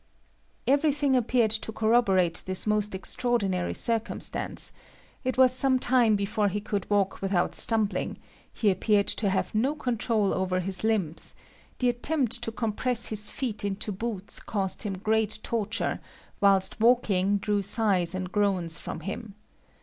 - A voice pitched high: Yes, high, 210 Hz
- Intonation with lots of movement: No, average, 3.3 semitones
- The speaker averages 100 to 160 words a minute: Yes, average, 140 wpm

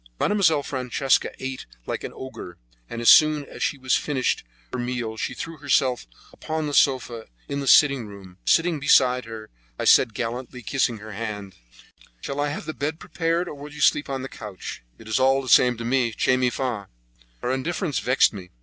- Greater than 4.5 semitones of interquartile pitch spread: No, average, 3.8 semitones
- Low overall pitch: Yes, low, 130 Hz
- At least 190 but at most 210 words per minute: Yes, average, 200 wpm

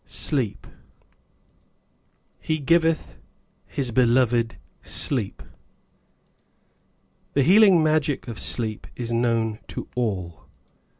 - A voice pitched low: Yes, low, 125 Hz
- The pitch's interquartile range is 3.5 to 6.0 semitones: Yes, average, 5.1 semitones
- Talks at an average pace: No, slow, 80 wpm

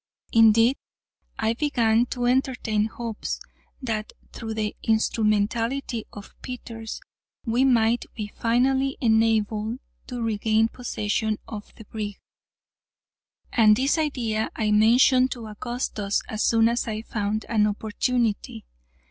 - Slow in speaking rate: Yes, slow, 115 wpm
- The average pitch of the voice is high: Yes, high, 225 Hz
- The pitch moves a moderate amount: No, narrow, 2.1 semitones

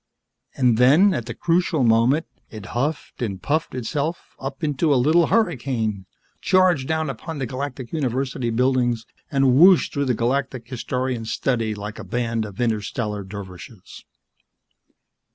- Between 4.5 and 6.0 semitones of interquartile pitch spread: No, average, 4.1 semitones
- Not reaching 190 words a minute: Yes, average, 140 wpm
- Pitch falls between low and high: No, low, 125 Hz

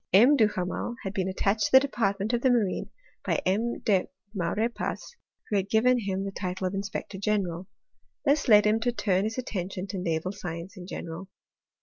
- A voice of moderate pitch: No, high, 200 Hz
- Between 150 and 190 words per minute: Yes, average, 185 wpm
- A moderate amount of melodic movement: Yes, average, 3.2 semitones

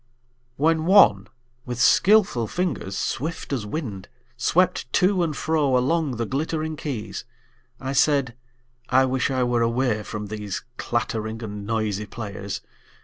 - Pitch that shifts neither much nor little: No, wide, 6.2 semitones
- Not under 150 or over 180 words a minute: No, slow, 135 wpm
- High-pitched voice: No, low, 125 Hz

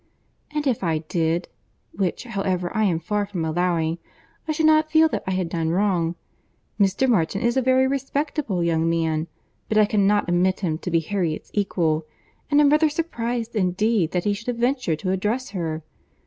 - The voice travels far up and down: Yes, wide, 6.2 semitones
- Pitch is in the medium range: No, high, 195 Hz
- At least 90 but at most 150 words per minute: No, average, 185 wpm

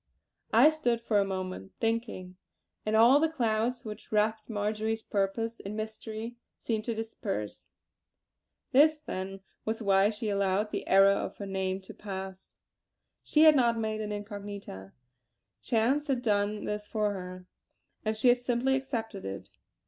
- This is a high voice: Yes, high, 215 Hz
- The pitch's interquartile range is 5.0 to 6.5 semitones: No, average, 2.8 semitones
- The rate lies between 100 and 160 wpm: Yes, average, 150 wpm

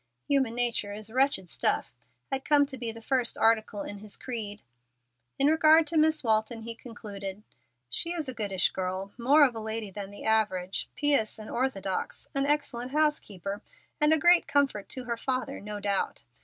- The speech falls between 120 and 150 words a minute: No, average, 180 wpm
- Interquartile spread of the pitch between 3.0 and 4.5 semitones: No, average, 5.2 semitones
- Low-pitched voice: No, high, 230 Hz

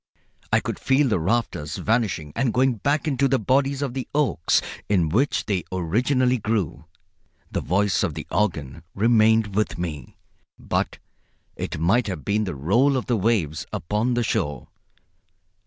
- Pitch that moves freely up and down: Yes, wide, 6.3 semitones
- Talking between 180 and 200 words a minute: No, average, 155 wpm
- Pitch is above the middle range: No, low, 110 Hz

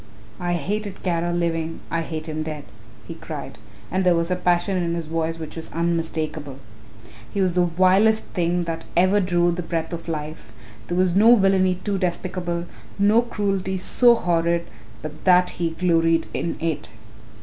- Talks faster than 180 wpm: No, average, 170 wpm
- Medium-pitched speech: Yes, medium, 175 Hz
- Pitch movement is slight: Yes, narrow, 2.1 semitones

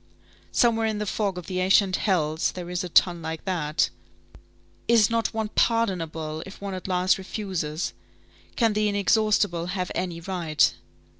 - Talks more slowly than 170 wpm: Yes, average, 155 wpm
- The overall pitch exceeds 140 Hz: Yes, medium, 185 Hz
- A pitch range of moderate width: Yes, average, 3.7 semitones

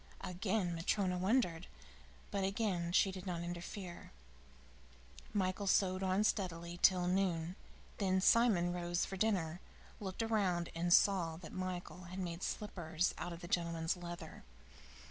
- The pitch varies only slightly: Yes, narrow, 2.0 semitones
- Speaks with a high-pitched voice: No, medium, 180 Hz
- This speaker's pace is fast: No, slow, 135 wpm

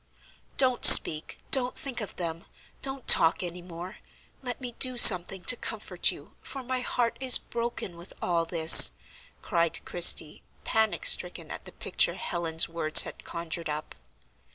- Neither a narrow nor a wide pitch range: No, wide, 6.7 semitones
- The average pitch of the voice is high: No, medium, 180 Hz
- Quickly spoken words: No, average, 155 wpm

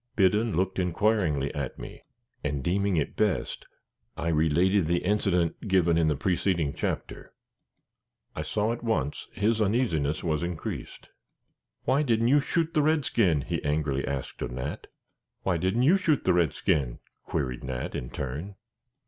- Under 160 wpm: Yes, average, 150 wpm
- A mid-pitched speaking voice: No, very low, 90 Hz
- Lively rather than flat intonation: Yes, wide, 6.4 semitones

